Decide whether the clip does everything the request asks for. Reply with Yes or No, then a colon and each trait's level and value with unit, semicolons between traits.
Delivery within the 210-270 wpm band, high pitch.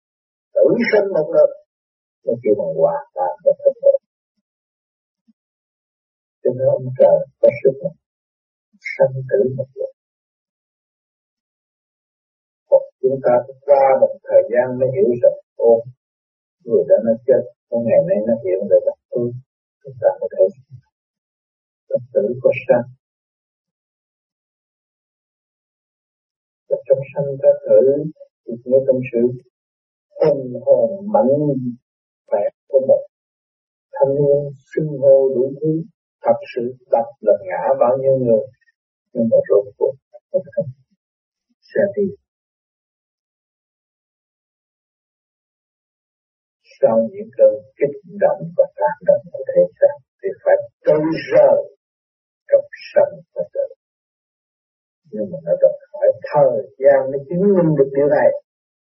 Yes: average, 240 wpm; very high, 260 Hz